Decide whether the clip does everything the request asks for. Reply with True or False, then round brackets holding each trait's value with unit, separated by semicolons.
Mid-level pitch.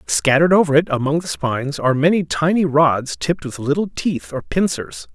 True (150 Hz)